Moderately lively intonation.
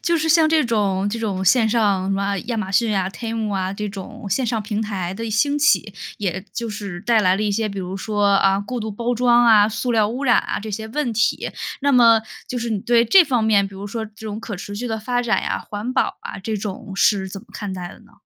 Yes: average, 3.0 semitones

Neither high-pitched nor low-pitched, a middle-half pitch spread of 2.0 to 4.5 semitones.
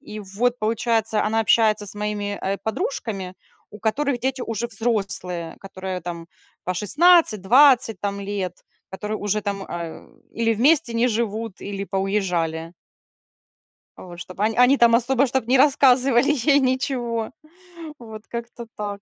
No: high, 220 Hz; average, 3.7 semitones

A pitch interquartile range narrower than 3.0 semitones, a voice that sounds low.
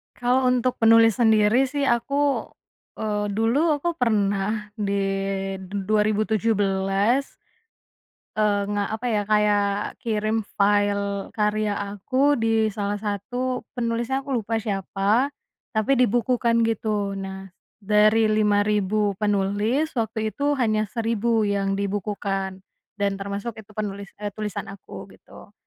No: narrow, 2.4 semitones; high, 215 Hz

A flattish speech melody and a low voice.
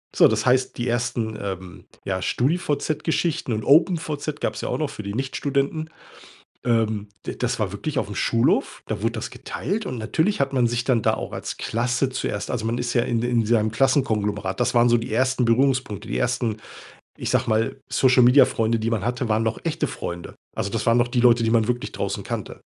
No: average, 3.1 semitones; low, 120 Hz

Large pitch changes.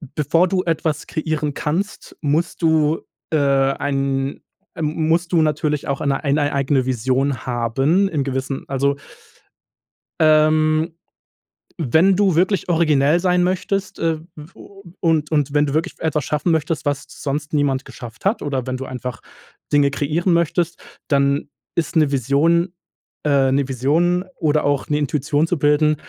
No: average, 3.0 semitones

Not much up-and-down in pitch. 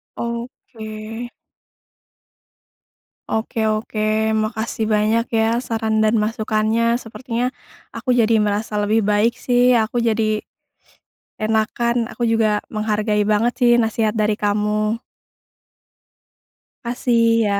Yes: narrow, 1.4 semitones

